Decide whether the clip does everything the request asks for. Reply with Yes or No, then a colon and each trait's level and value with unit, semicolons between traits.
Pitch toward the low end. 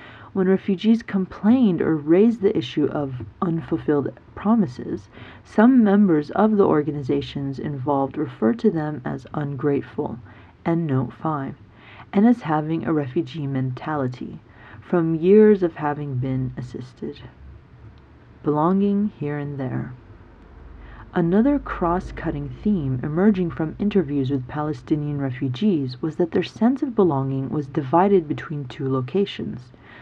No: medium, 150 Hz